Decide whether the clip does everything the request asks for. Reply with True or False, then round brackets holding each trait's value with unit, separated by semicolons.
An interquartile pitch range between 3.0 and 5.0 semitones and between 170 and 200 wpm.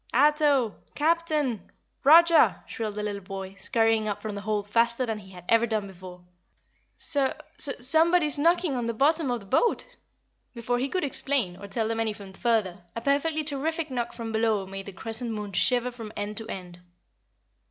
False (5.6 semitones; 180 wpm)